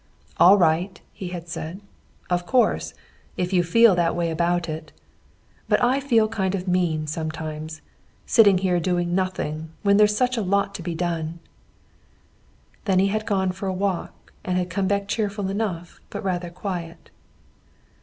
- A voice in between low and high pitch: Yes, medium, 180 Hz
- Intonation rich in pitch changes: No, average, 2.8 semitones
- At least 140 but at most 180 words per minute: Yes, average, 165 wpm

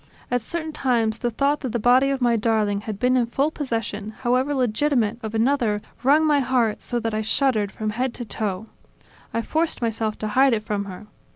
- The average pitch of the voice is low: No, high, 235 Hz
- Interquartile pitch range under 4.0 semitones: Yes, average, 3.5 semitones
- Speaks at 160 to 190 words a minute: No, fast, 205 wpm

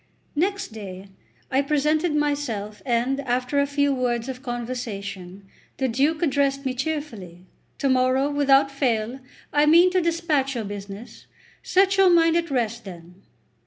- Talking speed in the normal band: Yes, average, 150 wpm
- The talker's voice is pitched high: Yes, very high, 270 Hz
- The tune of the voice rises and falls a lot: No, average, 4.4 semitones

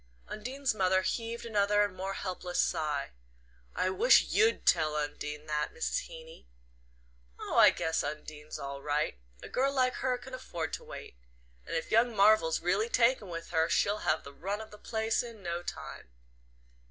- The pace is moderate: Yes, average, 170 wpm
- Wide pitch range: Yes, wide, 6.2 semitones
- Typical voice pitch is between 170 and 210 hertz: Yes, medium, 185 Hz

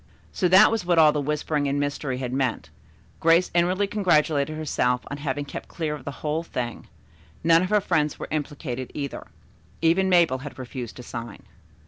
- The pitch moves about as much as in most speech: Yes, average, 4.0 semitones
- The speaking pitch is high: No, medium, 150 Hz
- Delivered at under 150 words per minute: No, average, 180 wpm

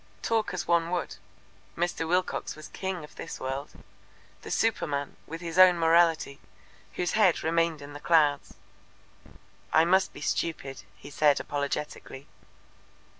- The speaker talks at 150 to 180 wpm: No, slow, 135 wpm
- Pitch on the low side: No, medium, 165 Hz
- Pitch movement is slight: No, average, 3.3 semitones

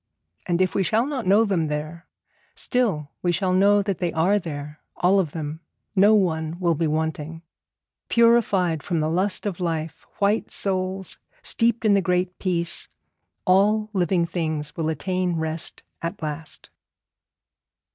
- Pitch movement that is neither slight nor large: Yes, average, 3.7 semitones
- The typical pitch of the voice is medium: Yes, medium, 180 Hz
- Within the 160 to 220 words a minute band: No, average, 150 wpm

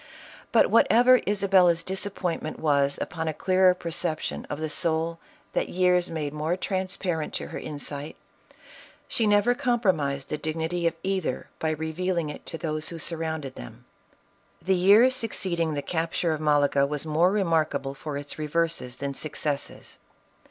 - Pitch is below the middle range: No, medium, 165 Hz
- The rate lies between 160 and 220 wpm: No, average, 150 wpm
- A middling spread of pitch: Yes, average, 3.4 semitones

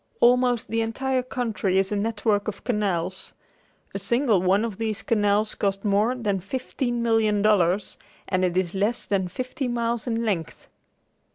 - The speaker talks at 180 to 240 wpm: No, average, 160 wpm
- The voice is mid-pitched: No, high, 215 Hz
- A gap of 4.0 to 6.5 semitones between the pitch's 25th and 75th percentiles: No, average, 3.2 semitones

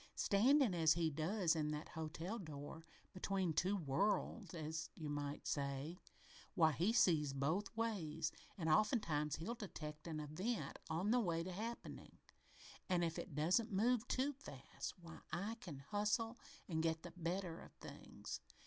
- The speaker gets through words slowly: No, average, 155 wpm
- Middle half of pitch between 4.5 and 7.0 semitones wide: Yes, average, 4.9 semitones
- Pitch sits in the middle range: Yes, medium, 170 Hz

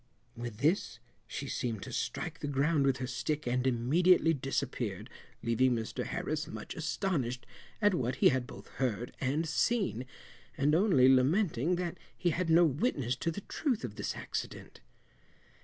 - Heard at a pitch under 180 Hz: Yes, low, 135 Hz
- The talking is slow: No, average, 155 wpm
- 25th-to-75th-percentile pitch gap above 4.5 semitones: Yes, average, 5.2 semitones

